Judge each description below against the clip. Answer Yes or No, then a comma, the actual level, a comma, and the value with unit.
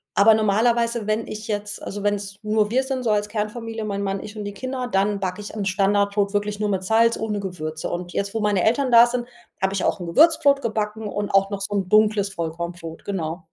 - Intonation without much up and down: Yes, narrow, 2.1 semitones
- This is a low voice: No, high, 205 Hz